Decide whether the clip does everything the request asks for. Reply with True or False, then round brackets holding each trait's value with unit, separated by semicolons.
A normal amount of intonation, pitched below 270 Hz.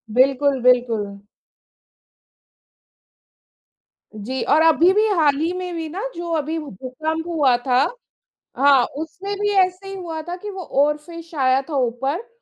False (4.8 semitones; 310 Hz)